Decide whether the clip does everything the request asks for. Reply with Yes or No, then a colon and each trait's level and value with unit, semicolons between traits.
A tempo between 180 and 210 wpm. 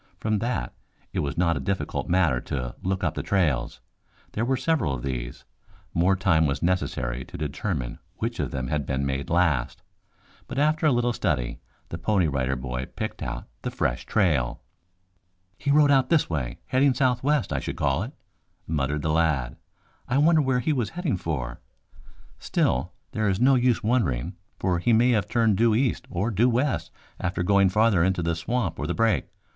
Yes: average, 185 wpm